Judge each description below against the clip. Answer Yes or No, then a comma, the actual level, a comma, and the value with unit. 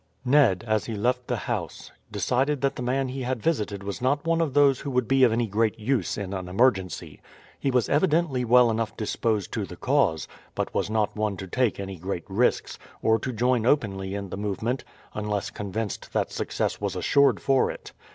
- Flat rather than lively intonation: No, average, 4.4 semitones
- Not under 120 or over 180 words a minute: No, average, 200 wpm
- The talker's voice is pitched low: Yes, low, 115 Hz